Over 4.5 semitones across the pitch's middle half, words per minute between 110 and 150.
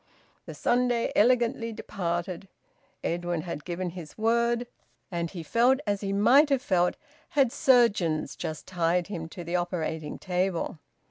Yes: wide, 5.5 semitones; average, 140 wpm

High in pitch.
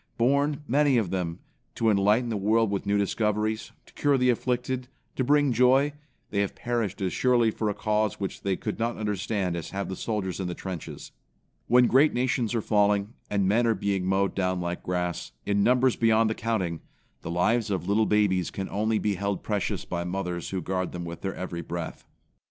No: low, 105 Hz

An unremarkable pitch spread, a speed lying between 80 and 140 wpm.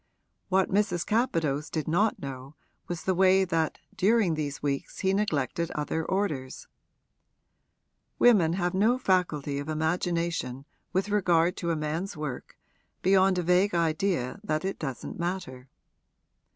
Yes: average, 3.9 semitones; slow, 135 wpm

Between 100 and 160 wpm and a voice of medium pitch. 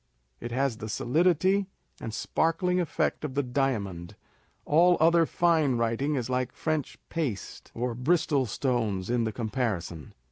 No: average, 140 wpm; low, 130 Hz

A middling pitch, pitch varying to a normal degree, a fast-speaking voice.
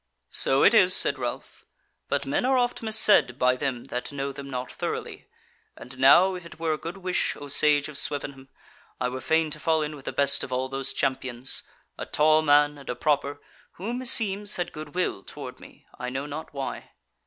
Yes: medium, 145 Hz; average, 4.1 semitones; fast, 210 wpm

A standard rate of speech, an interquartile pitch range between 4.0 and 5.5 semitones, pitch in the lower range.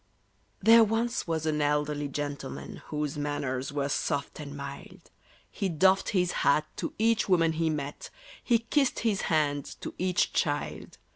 No: average, 150 wpm; average, 4.8 semitones; medium, 155 Hz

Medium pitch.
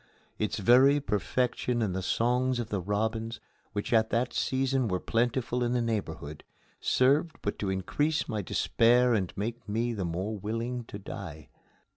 No: low, 115 Hz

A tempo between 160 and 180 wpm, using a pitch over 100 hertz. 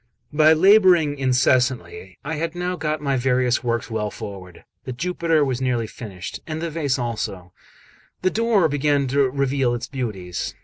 Yes: average, 165 wpm; low, 135 Hz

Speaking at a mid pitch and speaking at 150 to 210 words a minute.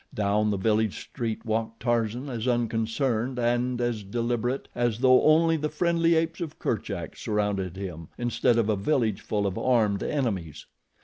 No: low, 115 Hz; average, 160 wpm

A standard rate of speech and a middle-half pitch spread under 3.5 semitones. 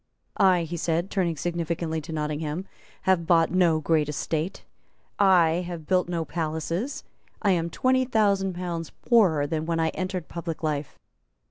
Yes: average, 150 wpm; narrow, 2.5 semitones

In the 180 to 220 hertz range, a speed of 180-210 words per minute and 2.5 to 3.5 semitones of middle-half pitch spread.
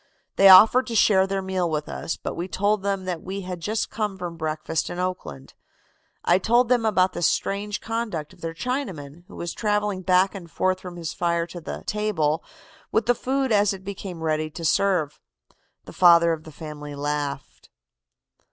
No: medium, 185 Hz; average, 190 wpm; average, 3.9 semitones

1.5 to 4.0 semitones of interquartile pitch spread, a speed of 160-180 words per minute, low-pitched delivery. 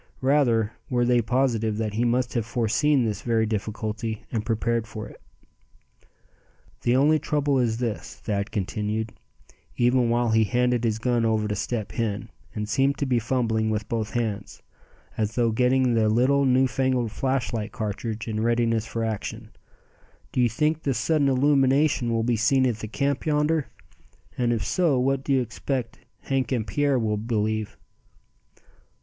Yes: average, 3.0 semitones; average, 165 wpm; low, 120 Hz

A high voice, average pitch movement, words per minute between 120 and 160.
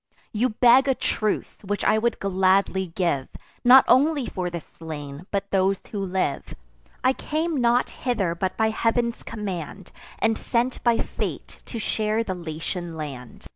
Yes: high, 200 Hz; average, 4.9 semitones; average, 155 wpm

